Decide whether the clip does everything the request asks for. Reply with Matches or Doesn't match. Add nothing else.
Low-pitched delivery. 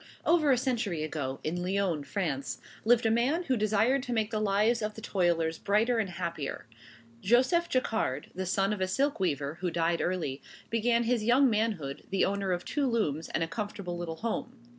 Doesn't match